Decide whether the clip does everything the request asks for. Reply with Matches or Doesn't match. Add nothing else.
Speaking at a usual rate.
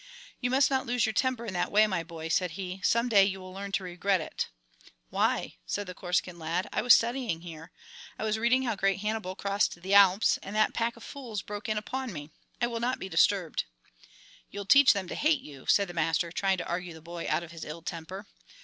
Doesn't match